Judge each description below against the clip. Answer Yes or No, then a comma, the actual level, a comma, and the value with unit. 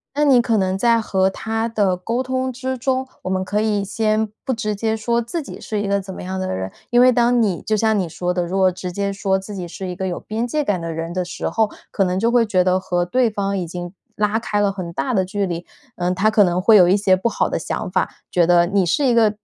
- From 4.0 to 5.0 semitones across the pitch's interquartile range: No, average, 3.6 semitones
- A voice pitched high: Yes, high, 200 Hz